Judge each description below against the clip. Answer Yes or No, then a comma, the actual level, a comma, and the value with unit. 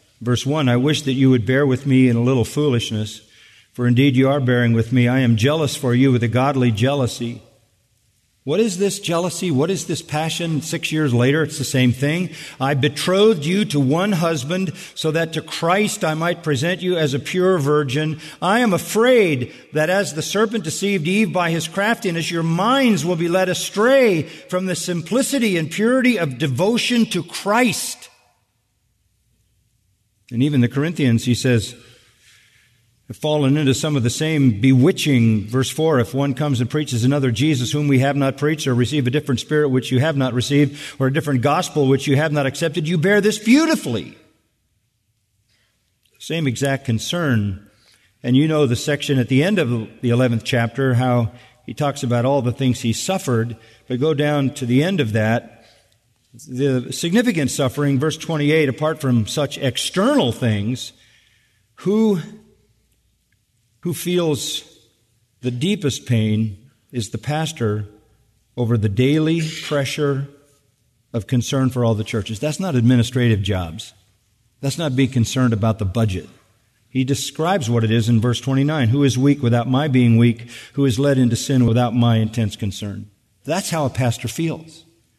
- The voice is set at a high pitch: No, low, 130 Hz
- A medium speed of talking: Yes, average, 170 wpm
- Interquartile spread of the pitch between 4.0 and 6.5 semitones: Yes, average, 5.0 semitones